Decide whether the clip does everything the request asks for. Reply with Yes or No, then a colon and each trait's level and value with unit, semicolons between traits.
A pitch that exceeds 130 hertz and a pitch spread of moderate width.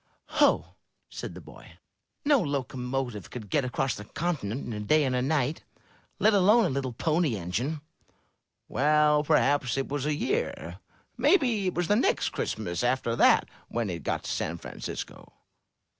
Yes: medium, 140 Hz; average, 4.9 semitones